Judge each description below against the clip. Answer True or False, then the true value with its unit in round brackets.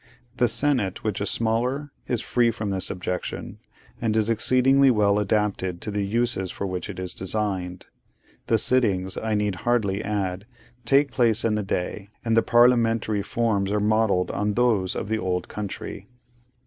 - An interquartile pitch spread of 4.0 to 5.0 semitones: False (3.2 semitones)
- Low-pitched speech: True (105 Hz)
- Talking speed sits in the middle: True (165 wpm)